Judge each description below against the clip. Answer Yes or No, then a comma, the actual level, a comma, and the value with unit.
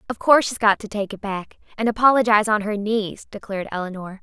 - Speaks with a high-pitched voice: Yes, high, 210 Hz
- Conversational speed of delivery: No, fast, 215 wpm